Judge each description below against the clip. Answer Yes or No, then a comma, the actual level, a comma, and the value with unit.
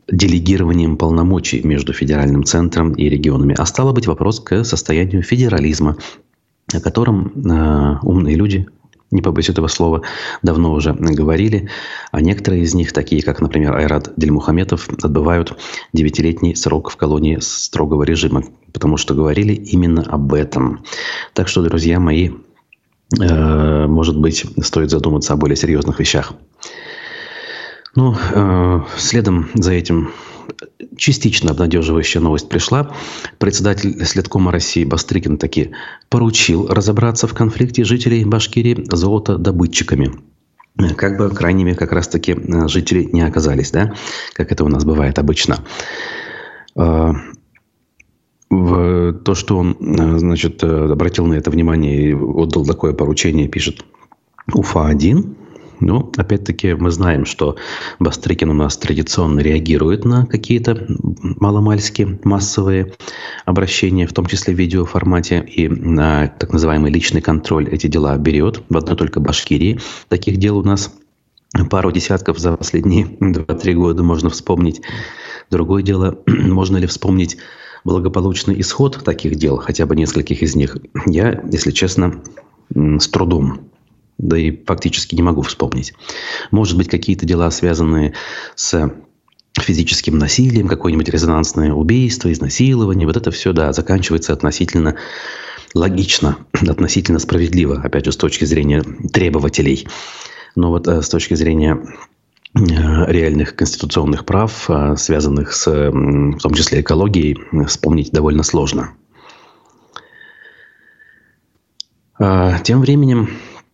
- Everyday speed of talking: Yes, average, 120 wpm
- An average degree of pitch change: Yes, average, 3.8 semitones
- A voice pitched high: No, very low, 85 Hz